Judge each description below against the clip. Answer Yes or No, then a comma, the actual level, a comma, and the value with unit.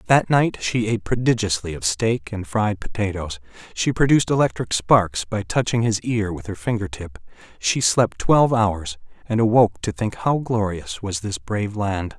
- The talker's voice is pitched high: No, low, 105 Hz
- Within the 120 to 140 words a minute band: No, average, 175 wpm